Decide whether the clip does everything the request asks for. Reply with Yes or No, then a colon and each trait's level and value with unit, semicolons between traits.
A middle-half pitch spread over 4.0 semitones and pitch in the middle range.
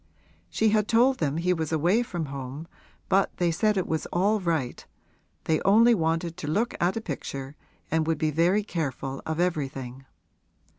Yes: average, 4.7 semitones; medium, 165 Hz